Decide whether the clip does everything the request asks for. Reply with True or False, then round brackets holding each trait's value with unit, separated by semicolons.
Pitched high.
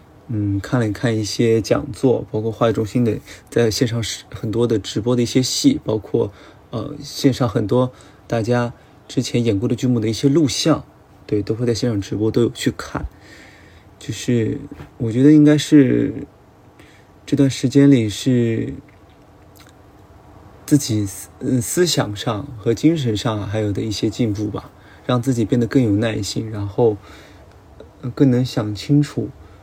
False (115 Hz)